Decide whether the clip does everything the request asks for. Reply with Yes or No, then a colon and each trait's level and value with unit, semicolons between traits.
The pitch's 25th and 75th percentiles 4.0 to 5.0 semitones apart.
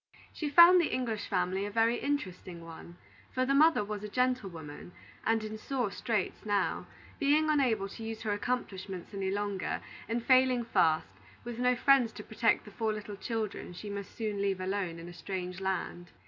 Yes: average, 4.4 semitones